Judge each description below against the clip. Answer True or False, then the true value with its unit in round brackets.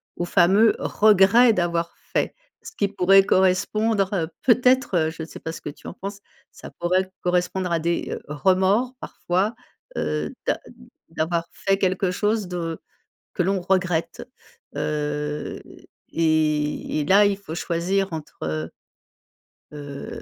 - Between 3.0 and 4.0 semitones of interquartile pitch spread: True (3.3 semitones)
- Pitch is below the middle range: False (180 Hz)